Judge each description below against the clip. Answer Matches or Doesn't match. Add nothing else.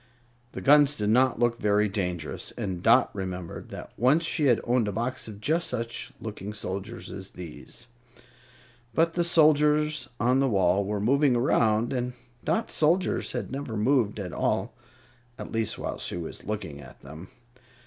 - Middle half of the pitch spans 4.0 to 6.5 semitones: Matches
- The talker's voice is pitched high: Doesn't match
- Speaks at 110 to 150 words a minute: Doesn't match